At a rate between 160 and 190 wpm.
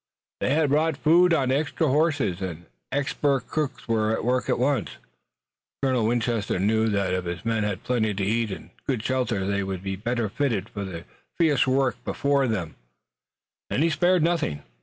Yes: average, 180 wpm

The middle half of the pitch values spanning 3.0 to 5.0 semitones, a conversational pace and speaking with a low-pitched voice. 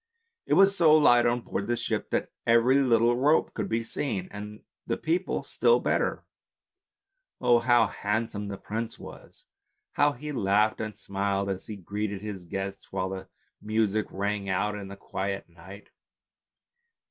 Yes: average, 3.5 semitones; average, 160 wpm; low, 105 Hz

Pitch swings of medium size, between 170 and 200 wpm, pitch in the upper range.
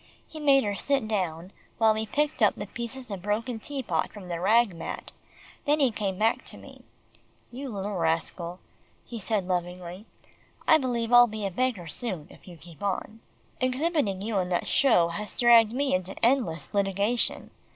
Yes: average, 4.9 semitones; average, 180 wpm; high, 210 Hz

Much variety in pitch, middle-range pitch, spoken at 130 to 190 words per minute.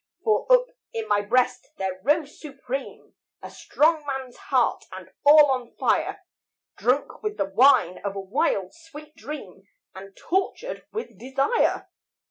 No: wide, 5.7 semitones; very high, 275 Hz; average, 140 wpm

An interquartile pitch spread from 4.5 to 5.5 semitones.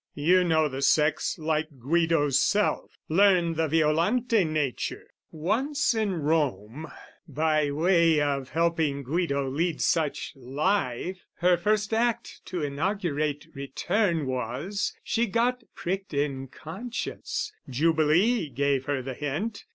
Yes: average, 4.8 semitones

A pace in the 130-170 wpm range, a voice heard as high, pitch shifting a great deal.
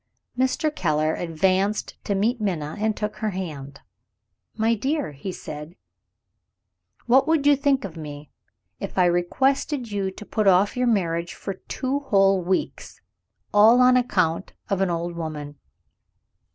Yes: average, 150 wpm; high, 195 Hz; wide, 6.2 semitones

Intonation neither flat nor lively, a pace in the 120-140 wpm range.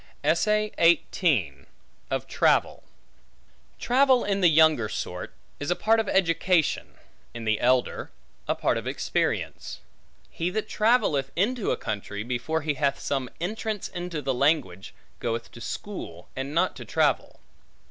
No: wide, 7.7 semitones; slow, 135 wpm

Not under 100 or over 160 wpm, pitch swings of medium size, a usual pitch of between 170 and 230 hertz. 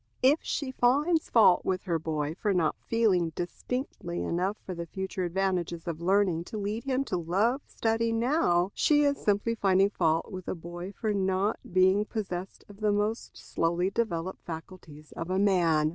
No: average, 170 wpm; average, 4.2 semitones; high, 190 Hz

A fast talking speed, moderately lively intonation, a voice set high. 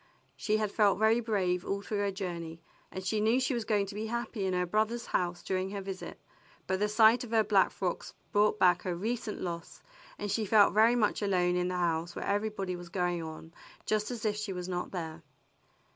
Yes: fast, 220 wpm; average, 3.3 semitones; high, 200 Hz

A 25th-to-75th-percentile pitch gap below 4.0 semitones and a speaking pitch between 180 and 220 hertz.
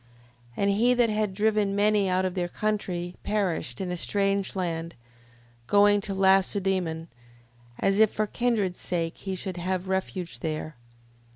Yes: narrow, 2.6 semitones; high, 190 Hz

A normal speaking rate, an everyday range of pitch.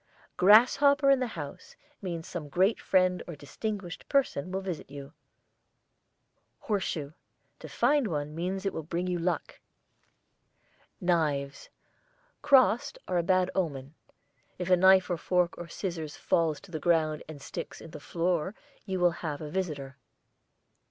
Yes: average, 145 wpm; average, 3.6 semitones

